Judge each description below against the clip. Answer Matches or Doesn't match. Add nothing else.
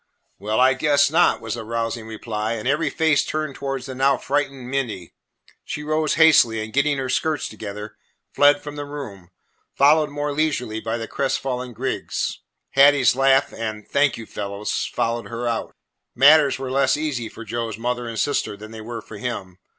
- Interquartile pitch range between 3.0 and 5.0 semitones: Matches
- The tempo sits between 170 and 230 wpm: Matches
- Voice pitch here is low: Matches